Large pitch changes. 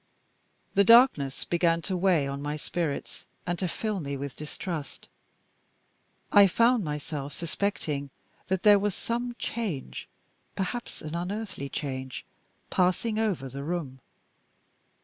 Yes: wide, 6.0 semitones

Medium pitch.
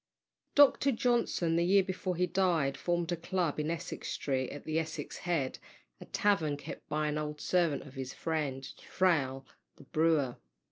Yes: medium, 160 Hz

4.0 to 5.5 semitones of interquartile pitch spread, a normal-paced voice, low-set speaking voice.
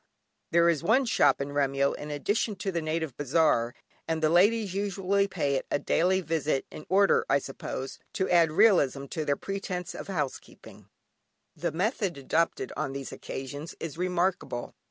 No: average, 5.0 semitones; average, 165 wpm; medium, 165 Hz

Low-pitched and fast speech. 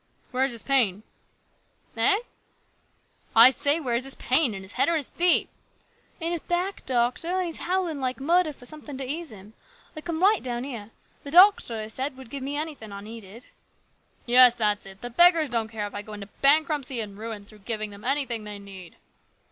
No: very high, 255 Hz; fast, 220 wpm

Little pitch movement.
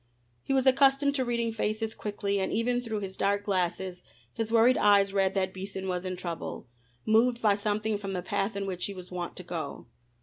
No: average, 3.2 semitones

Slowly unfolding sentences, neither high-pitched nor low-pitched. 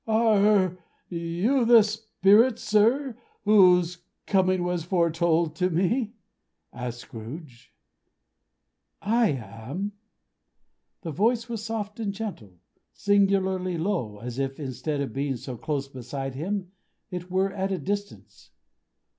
Yes: slow, 115 wpm; medium, 180 Hz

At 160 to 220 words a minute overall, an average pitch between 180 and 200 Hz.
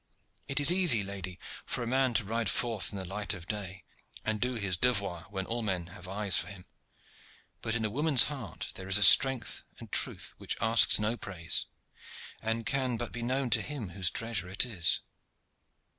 No: average, 195 wpm; low, 110 Hz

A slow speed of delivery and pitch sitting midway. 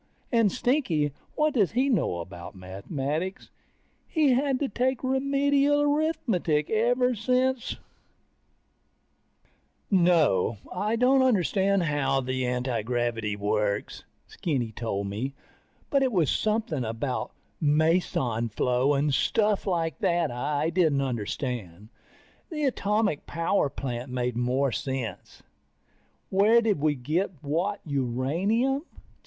Yes: slow, 115 wpm; medium, 160 Hz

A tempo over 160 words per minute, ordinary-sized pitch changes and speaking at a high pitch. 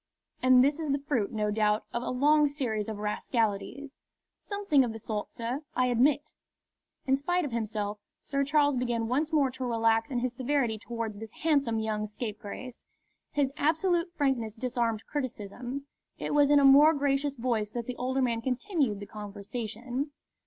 Yes: average, 170 wpm; average, 4.2 semitones; very high, 250 Hz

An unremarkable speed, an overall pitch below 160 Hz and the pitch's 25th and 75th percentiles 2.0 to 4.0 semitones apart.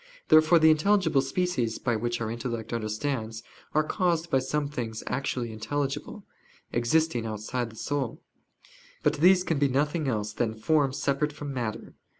No: average, 150 wpm; low, 135 Hz; average, 5.0 semitones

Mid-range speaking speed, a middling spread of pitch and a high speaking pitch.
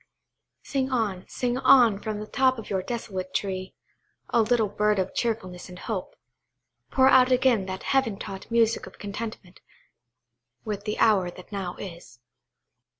Yes: average, 150 wpm; average, 4.0 semitones; high, 210 Hz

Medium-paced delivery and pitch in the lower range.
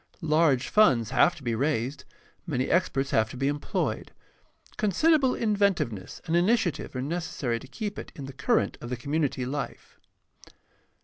No: average, 165 wpm; medium, 145 Hz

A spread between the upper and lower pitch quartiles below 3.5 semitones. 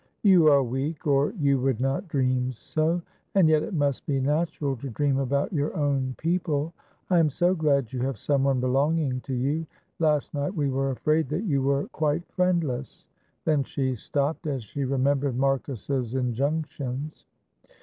Yes: average, 2.8 semitones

